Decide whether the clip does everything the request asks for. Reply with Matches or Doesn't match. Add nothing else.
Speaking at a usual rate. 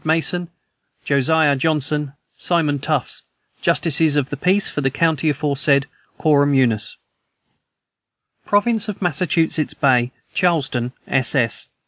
Doesn't match